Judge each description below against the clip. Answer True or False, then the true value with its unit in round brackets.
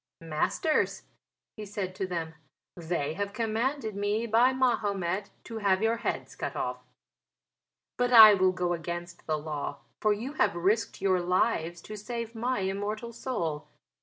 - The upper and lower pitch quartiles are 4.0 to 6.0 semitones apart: True (4.5 semitones)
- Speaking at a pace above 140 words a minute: True (150 wpm)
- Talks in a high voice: True (200 Hz)